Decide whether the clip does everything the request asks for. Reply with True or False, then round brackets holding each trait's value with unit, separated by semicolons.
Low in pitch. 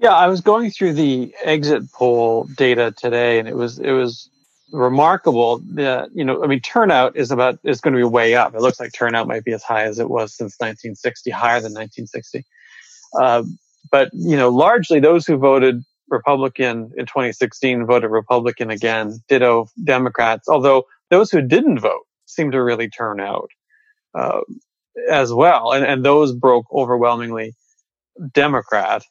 True (125 Hz)